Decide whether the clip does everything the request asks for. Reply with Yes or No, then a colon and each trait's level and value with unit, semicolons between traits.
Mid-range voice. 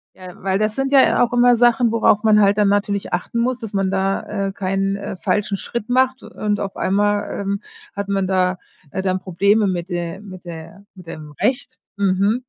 No: high, 200 Hz